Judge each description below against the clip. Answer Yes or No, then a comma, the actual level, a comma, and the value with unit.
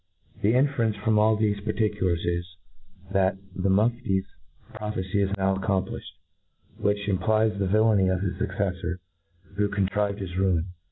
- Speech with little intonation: Yes, narrow, 2.1 semitones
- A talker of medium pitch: No, low, 100 Hz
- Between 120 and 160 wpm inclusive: Yes, slow, 135 wpm